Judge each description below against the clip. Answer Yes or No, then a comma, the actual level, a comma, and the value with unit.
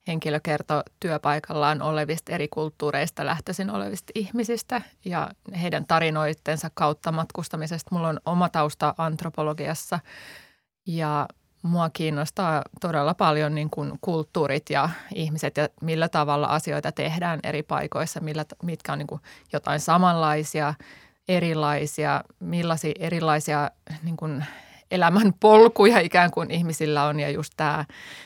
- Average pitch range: No, narrow, 2.1 semitones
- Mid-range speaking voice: Yes, medium, 155 Hz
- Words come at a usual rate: Yes, average, 115 wpm